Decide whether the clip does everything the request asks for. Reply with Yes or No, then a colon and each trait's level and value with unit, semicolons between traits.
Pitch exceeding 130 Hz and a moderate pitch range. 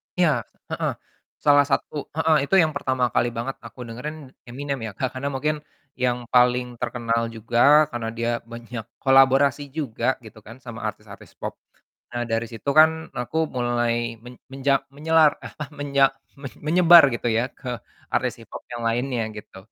No: low, 125 Hz; average, 3.4 semitones